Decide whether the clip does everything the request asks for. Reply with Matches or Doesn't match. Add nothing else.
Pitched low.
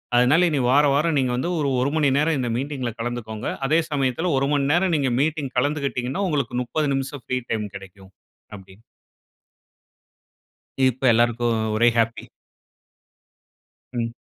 Matches